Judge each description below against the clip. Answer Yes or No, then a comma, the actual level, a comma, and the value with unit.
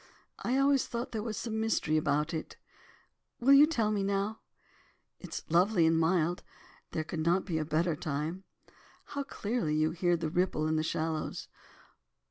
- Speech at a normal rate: Yes, average, 175 wpm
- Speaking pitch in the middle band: Yes, medium, 175 Hz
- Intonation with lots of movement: Yes, wide, 5.8 semitones